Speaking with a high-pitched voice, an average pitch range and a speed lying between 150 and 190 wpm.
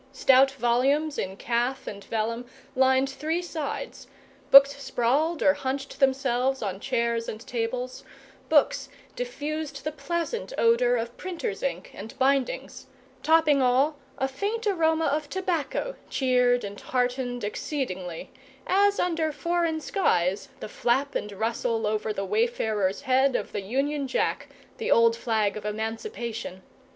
No: very high, 260 Hz; average, 4.9 semitones; slow, 135 wpm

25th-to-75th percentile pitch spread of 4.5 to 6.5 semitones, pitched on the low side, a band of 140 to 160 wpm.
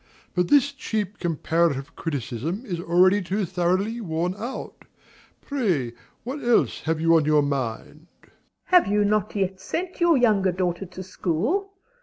No: average, 5.0 semitones; medium, 185 Hz; average, 155 wpm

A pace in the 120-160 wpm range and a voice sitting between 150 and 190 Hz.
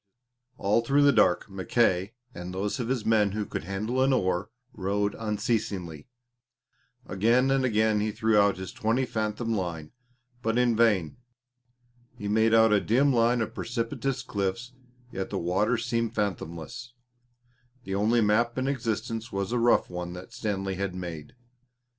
No: average, 155 wpm; low, 110 Hz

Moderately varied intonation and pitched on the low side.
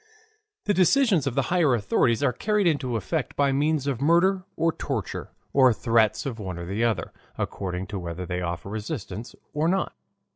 No: wide, 7.7 semitones; low, 130 Hz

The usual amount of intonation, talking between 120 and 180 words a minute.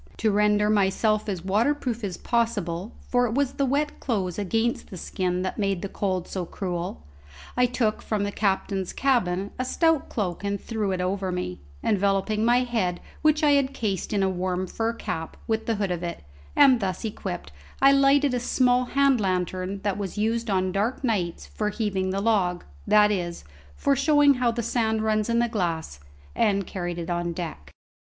No: average, 4.3 semitones; average, 190 wpm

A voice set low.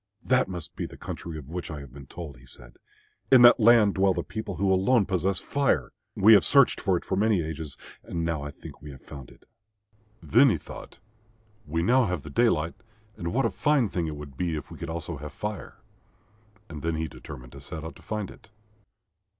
Yes: very low, 85 Hz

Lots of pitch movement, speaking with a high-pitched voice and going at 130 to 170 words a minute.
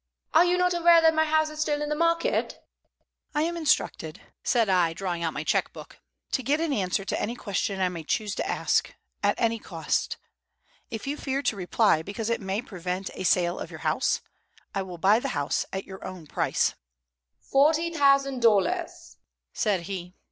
No: wide, 8.5 semitones; high, 225 Hz; average, 190 wpm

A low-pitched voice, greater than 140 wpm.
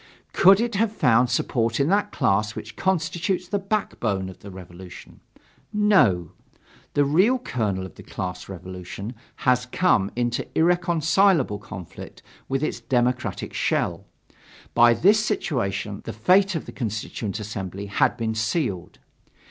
No: low, 120 Hz; slow, 135 wpm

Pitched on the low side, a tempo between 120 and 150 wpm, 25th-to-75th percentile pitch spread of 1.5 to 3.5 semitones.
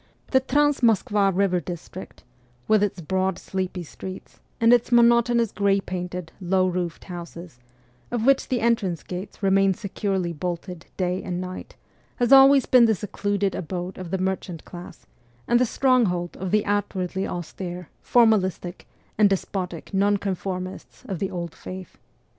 No: high, 190 Hz; average, 145 wpm; average, 3.0 semitones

